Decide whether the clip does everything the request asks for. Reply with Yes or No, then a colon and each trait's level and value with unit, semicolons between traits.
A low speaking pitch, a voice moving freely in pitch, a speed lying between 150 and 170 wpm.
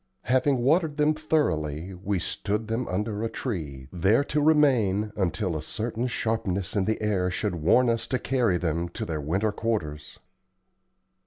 Yes: low, 105 Hz; wide, 5.8 semitones; average, 160 wpm